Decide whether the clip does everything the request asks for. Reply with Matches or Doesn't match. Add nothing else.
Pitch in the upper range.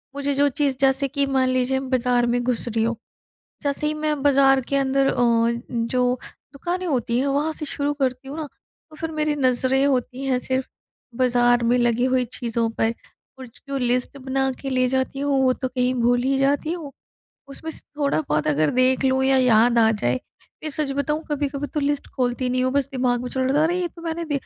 Matches